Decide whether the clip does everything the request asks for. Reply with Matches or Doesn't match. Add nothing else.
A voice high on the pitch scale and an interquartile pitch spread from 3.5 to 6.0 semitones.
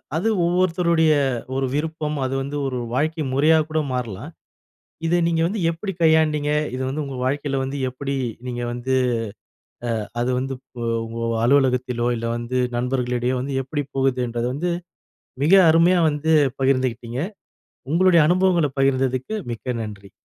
Doesn't match